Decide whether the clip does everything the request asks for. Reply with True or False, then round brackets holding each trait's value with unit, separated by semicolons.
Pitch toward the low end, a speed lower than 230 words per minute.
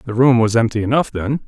False (120 Hz; 245 wpm)